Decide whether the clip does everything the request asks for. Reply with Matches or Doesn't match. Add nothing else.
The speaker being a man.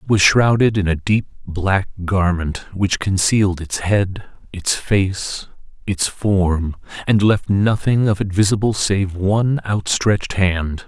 Matches